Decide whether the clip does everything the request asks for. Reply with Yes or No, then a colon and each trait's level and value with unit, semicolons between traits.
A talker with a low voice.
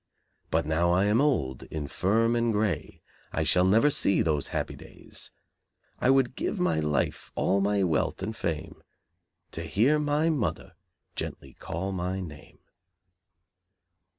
Yes: very low, 95 Hz